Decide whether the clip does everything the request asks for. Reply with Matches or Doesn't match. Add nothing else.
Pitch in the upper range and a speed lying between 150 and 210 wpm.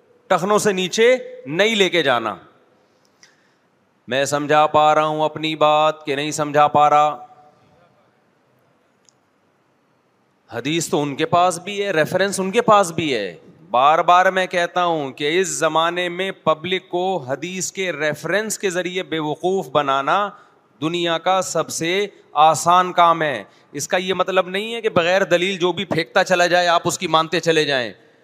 Doesn't match